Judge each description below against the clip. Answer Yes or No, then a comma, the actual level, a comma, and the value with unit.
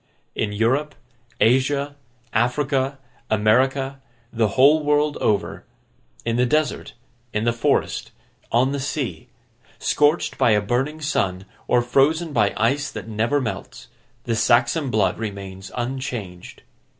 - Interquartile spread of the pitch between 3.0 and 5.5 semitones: Yes, average, 4.5 semitones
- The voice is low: Yes, low, 125 Hz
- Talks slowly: Yes, slow, 125 wpm